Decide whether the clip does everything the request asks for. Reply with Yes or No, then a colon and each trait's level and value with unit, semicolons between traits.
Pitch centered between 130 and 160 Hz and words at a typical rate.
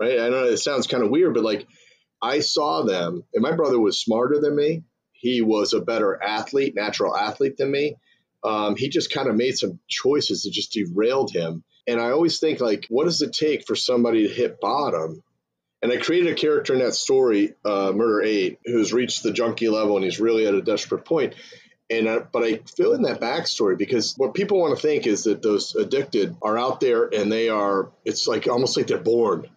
No: low, 135 Hz; fast, 220 wpm